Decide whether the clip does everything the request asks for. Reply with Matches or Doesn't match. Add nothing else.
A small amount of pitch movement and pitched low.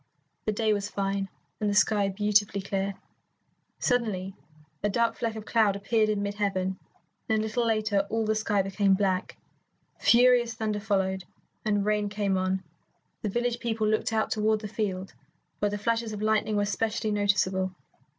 Doesn't match